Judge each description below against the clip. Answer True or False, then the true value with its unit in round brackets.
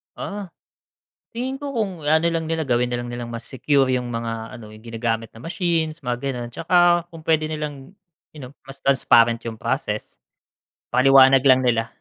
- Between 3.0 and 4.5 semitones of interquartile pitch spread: False (5.2 semitones)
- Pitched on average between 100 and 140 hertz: True (135 Hz)